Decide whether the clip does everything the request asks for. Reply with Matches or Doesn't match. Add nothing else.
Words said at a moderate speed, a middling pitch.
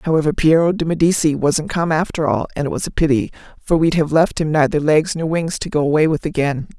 Doesn't match